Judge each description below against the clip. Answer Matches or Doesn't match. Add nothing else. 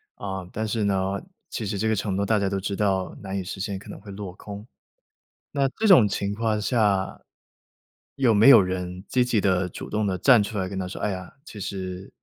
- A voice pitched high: Doesn't match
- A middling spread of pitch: Doesn't match